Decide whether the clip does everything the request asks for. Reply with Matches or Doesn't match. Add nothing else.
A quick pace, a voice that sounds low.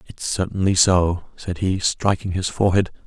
Doesn't match